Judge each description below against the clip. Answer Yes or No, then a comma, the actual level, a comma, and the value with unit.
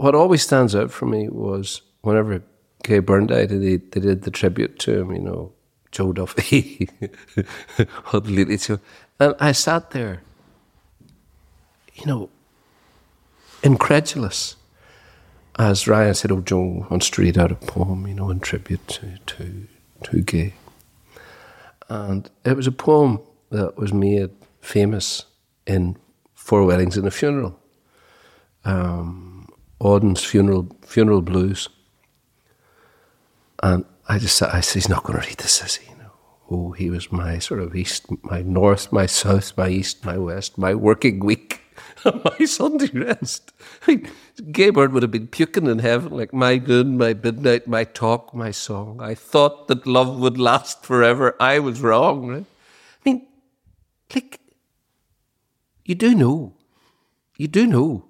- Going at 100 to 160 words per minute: Yes, average, 145 wpm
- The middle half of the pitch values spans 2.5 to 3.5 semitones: No, average, 5.2 semitones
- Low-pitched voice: Yes, low, 105 Hz